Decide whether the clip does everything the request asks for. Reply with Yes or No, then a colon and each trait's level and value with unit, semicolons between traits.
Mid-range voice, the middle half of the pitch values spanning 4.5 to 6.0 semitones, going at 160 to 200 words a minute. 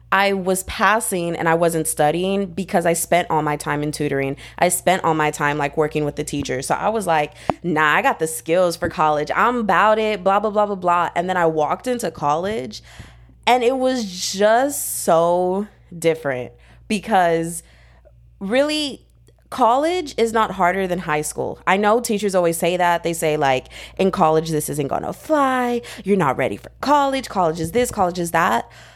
Yes: medium, 175 Hz; average, 5.1 semitones; average, 190 wpm